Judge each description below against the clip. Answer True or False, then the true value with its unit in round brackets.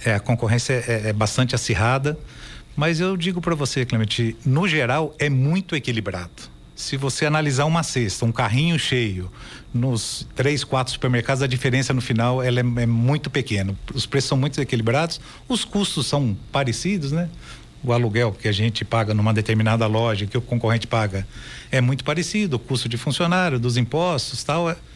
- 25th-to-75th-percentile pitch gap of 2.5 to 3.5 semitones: False (4.2 semitones)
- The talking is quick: False (175 wpm)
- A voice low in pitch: True (130 Hz)